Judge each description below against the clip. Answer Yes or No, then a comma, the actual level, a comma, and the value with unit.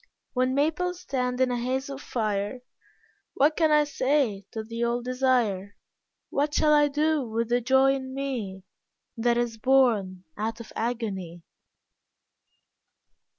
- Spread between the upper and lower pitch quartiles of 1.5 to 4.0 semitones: Yes, average, 3.6 semitones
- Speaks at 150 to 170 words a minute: No, average, 140 wpm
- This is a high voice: Yes, very high, 250 Hz